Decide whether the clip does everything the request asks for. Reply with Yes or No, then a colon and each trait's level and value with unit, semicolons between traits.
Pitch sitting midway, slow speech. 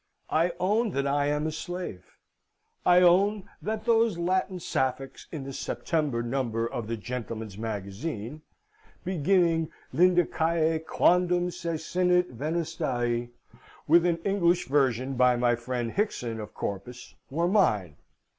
Yes: medium, 155 Hz; slow, 125 wpm